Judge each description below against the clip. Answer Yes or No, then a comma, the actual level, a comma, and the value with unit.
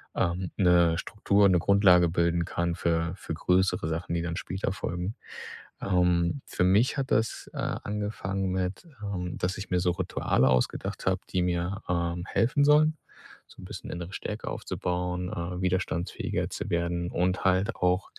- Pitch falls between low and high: No, very low, 90 Hz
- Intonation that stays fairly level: Yes, narrow, 2.1 semitones